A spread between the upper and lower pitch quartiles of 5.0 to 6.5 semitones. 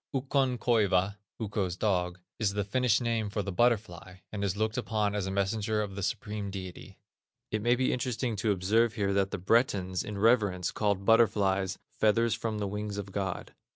No: narrow, 2.6 semitones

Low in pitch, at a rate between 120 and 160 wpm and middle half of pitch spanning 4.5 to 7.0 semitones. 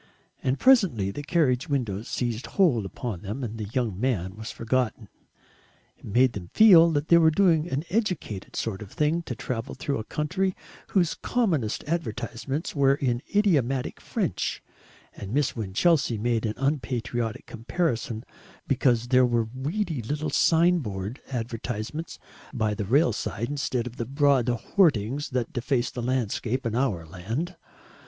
Yes: low, 125 Hz; average, 150 wpm; average, 5.1 semitones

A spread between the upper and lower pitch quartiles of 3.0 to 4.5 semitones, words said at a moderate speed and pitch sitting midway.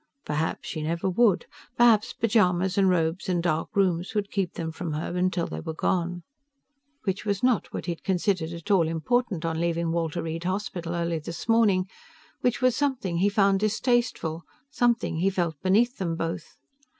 Yes: average, 3.6 semitones; average, 175 wpm; medium, 180 Hz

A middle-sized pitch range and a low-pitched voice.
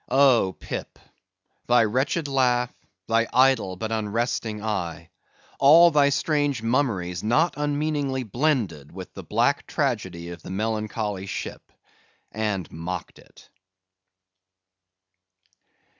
No: wide, 6.2 semitones; low, 115 Hz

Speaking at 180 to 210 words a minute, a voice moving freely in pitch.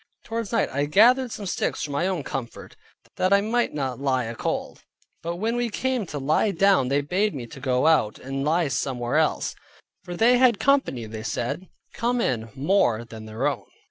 Yes: average, 200 wpm; wide, 8.4 semitones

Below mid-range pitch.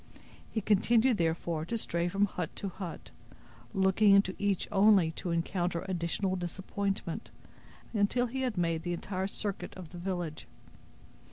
No: high, 190 Hz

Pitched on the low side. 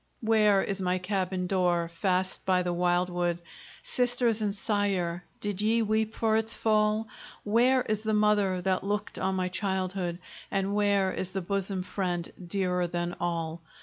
No: high, 190 Hz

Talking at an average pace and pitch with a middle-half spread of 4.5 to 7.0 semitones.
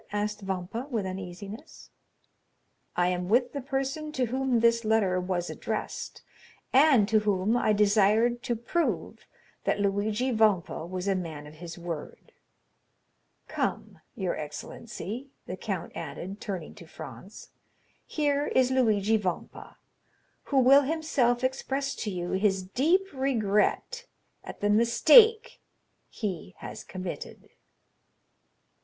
No: slow, 125 wpm; wide, 5.6 semitones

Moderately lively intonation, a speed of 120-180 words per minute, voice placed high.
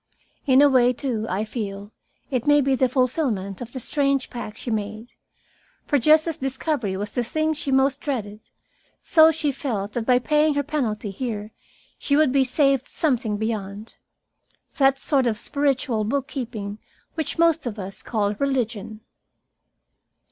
Yes: average, 4.7 semitones; average, 160 wpm; very high, 255 Hz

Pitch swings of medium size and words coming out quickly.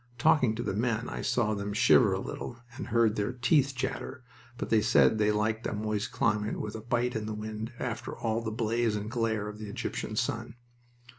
No: narrow, 2.0 semitones; fast, 210 wpm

